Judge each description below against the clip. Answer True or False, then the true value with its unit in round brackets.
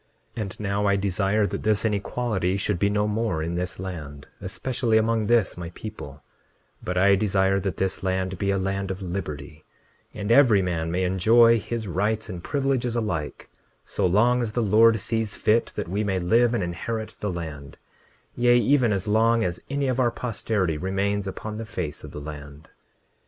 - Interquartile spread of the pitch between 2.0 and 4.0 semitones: True (3.7 semitones)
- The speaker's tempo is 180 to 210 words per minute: True (185 wpm)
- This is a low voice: True (100 Hz)